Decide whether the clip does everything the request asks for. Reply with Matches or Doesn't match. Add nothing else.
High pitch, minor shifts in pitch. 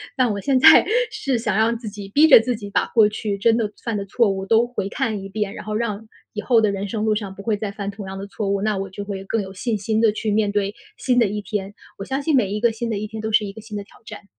Matches